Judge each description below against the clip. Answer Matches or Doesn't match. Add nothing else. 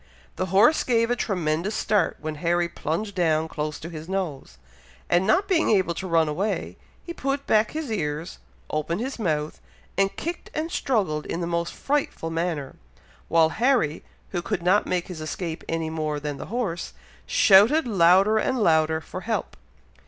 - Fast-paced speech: Doesn't match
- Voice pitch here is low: Doesn't match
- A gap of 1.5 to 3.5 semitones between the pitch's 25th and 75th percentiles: Doesn't match